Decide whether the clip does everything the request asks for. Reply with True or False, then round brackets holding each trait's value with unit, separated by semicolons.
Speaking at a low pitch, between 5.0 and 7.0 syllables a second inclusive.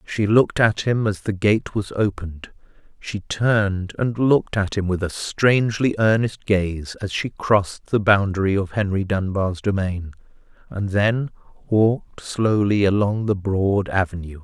False (100 Hz; 4.4 syllables/s)